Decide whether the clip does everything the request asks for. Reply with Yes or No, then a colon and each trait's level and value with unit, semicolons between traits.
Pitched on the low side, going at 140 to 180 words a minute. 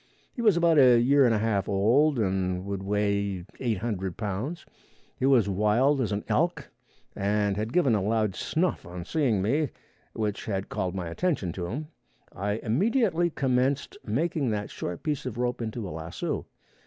Yes: low, 110 Hz; average, 170 wpm